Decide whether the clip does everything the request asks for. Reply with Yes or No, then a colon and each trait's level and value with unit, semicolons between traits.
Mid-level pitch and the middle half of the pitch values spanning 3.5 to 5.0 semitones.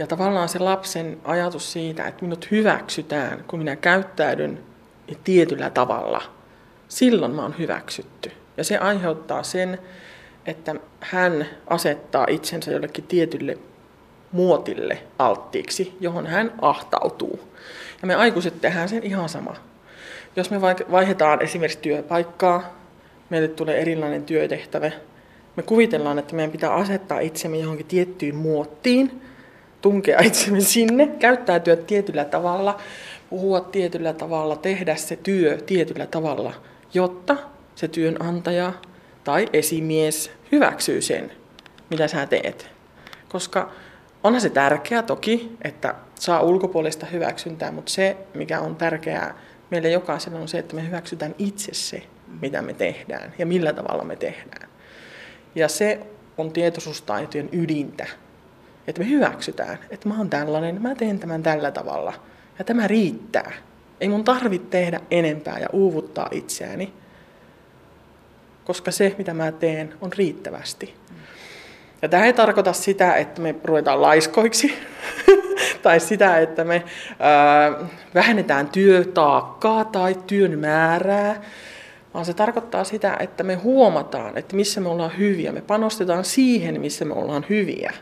Yes: medium, 175 Hz; average, 4.0 semitones